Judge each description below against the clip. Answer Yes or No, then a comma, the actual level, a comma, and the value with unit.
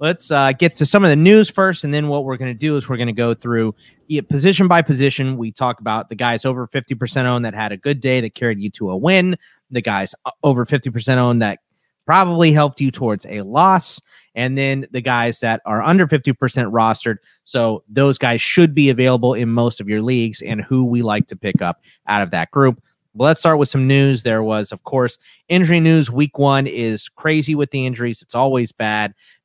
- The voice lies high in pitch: No, low, 130 Hz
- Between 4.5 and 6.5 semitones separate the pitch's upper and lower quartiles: No, average, 3.9 semitones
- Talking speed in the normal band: No, fast, 225 wpm